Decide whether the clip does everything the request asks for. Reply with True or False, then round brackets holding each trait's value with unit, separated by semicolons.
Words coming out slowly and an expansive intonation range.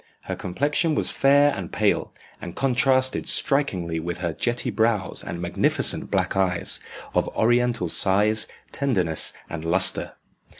True (130 wpm; 6.8 semitones)